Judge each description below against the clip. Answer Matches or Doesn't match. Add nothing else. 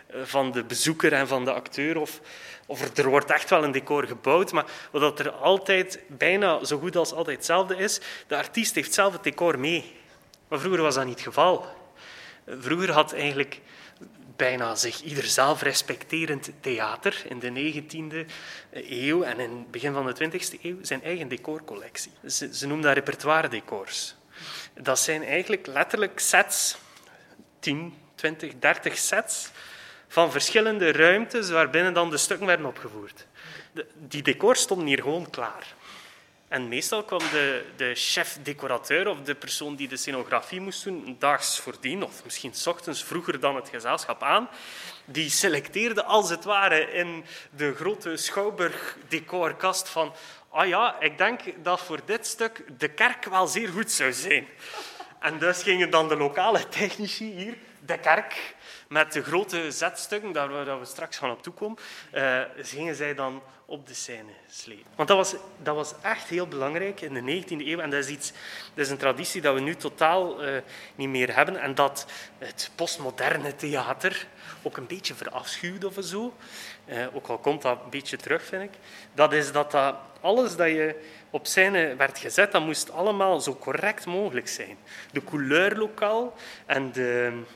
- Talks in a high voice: Doesn't match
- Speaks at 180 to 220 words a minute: Doesn't match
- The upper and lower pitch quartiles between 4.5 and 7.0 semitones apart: Matches